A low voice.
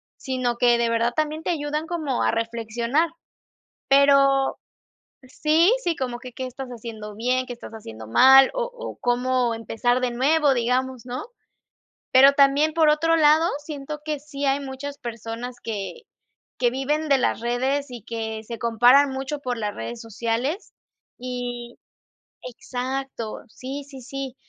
No: very high, 255 Hz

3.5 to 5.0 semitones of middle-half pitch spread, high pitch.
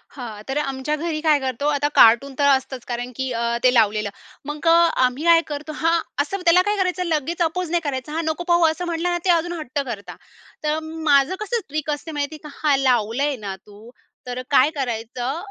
Yes: average, 4.3 semitones; very high, 295 Hz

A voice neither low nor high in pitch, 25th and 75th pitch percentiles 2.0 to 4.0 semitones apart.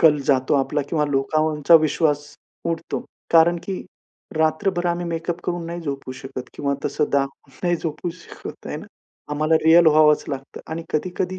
Yes: medium, 155 Hz; average, 2.8 semitones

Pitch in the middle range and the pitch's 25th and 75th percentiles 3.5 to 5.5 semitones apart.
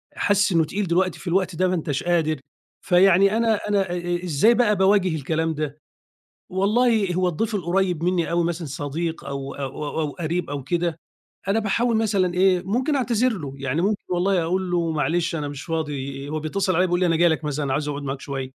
Yes: medium, 175 Hz; average, 3.9 semitones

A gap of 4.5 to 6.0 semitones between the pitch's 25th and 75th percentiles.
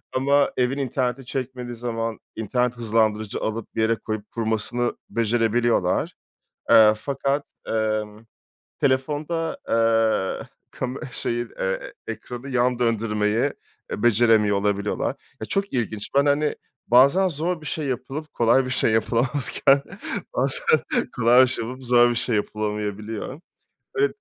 No: average, 3.3 semitones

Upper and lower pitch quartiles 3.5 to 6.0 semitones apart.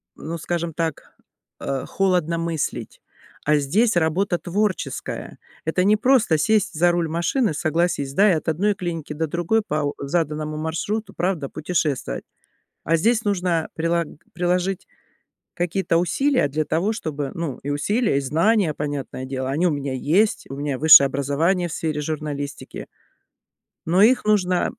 Yes: average, 3.8 semitones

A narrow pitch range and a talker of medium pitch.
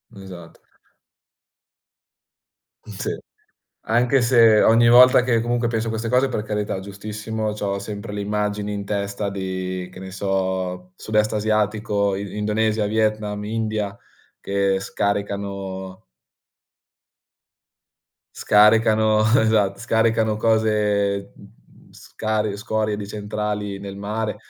No: narrow, 1.7 semitones; low, 105 Hz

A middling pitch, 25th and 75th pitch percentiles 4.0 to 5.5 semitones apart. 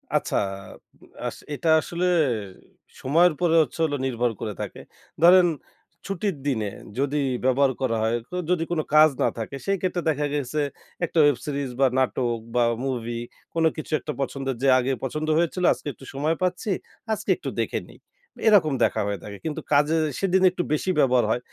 Yes: medium, 145 Hz; average, 4.7 semitones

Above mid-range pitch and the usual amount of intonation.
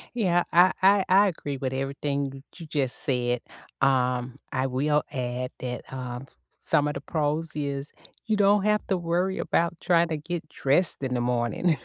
No: medium, 145 Hz; average, 5.0 semitones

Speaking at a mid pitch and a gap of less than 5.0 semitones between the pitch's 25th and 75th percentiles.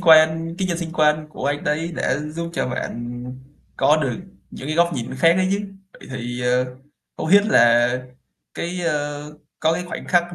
Yes: medium, 155 Hz; average, 4.4 semitones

